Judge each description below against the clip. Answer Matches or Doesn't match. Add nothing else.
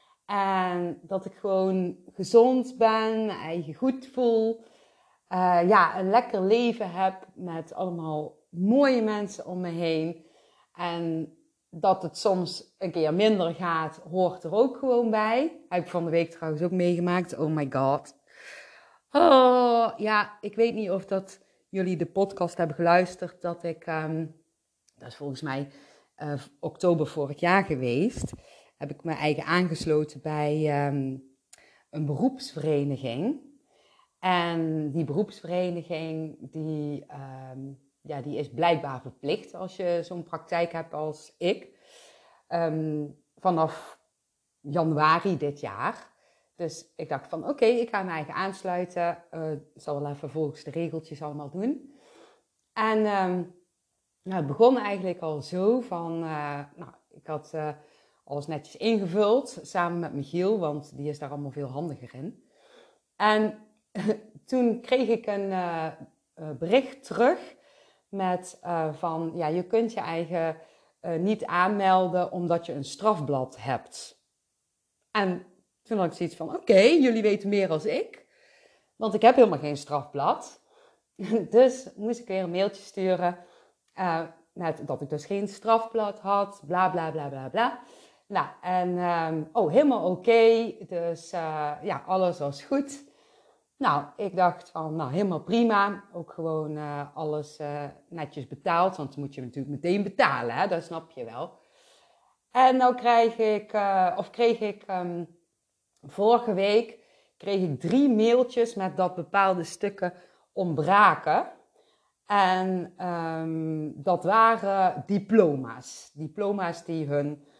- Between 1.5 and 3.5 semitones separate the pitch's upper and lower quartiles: Doesn't match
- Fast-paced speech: Doesn't match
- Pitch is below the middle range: Doesn't match